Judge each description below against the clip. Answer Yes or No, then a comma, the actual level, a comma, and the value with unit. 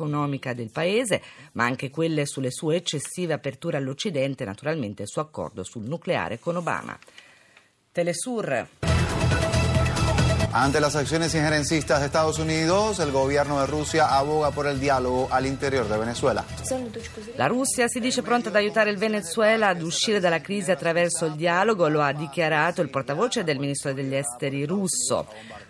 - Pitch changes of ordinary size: Yes, average, 4.3 semitones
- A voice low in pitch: No, medium, 155 Hz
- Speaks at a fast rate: No, average, 150 wpm